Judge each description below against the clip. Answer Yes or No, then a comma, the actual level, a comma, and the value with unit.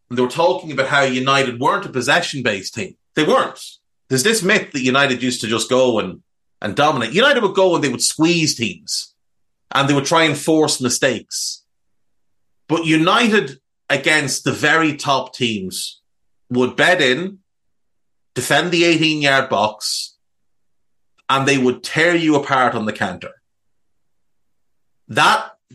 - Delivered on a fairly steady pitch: No, average, 4.2 semitones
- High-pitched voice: No, low, 135 Hz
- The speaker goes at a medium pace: Yes, average, 155 wpm